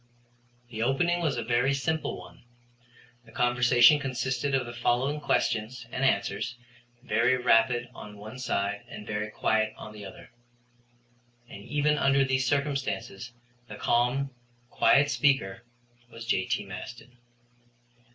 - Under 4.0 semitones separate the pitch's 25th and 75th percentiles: Yes, average, 3.5 semitones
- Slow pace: Yes, slow, 130 wpm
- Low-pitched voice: Yes, low, 120 Hz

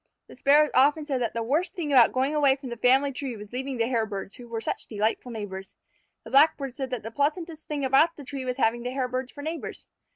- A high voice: Yes, very high, 260 Hz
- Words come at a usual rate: No, fast, 235 wpm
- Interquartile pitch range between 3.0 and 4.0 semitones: Yes, average, 3.4 semitones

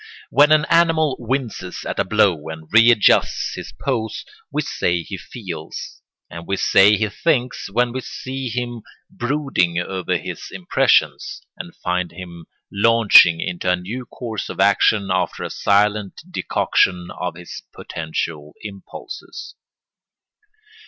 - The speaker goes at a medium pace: No, slow, 130 wpm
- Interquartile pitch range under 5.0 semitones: No, wide, 5.4 semitones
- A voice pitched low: Yes, low, 100 Hz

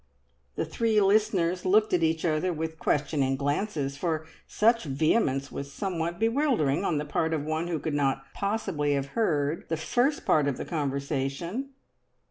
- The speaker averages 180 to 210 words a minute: No, average, 160 wpm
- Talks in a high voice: No, medium, 160 Hz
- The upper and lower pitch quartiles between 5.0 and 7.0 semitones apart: Yes, wide, 5.5 semitones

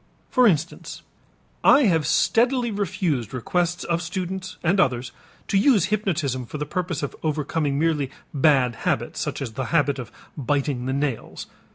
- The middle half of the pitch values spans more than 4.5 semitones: Yes, average, 5.2 semitones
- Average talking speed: Yes, average, 155 wpm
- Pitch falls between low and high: Yes, medium, 155 Hz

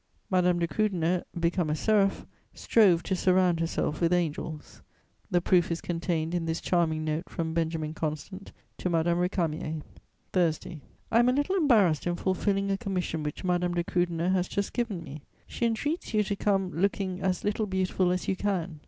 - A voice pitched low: No, medium, 180 Hz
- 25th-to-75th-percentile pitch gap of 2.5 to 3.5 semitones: Yes, average, 2.8 semitones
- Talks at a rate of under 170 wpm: No, average, 180 wpm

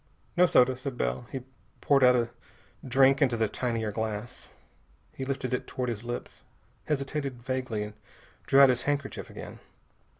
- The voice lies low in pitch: Yes, low, 125 Hz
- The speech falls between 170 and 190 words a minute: No, average, 160 wpm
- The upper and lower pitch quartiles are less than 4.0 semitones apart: Yes, narrow, 2.6 semitones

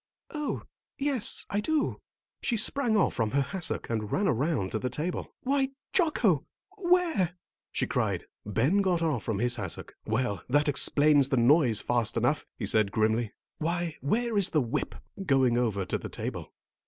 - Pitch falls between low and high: Yes, medium, 150 Hz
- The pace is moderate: Yes, average, 170 wpm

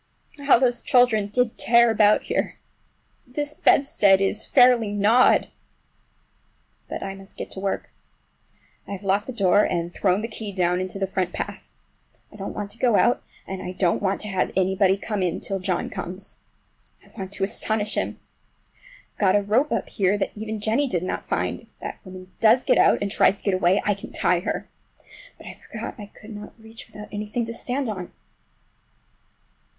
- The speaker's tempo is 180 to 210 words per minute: Yes, average, 190 wpm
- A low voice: No, high, 205 Hz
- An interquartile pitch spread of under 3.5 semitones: Yes, average, 2.9 semitones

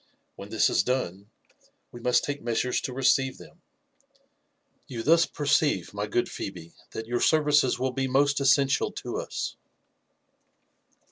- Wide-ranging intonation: No, average, 3.9 semitones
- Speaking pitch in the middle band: No, low, 130 Hz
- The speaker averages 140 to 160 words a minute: Yes, average, 145 wpm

